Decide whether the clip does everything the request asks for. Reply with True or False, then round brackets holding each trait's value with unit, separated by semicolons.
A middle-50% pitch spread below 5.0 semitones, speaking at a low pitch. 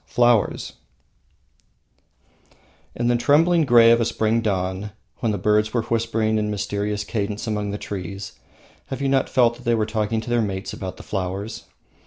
True (2.5 semitones; 110 Hz)